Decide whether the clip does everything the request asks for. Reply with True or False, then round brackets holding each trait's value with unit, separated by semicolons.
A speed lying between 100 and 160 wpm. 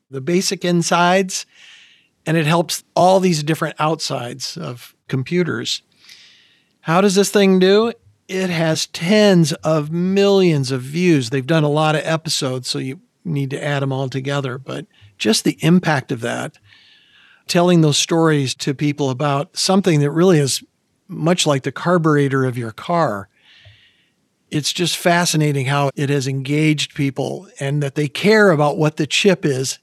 True (155 wpm)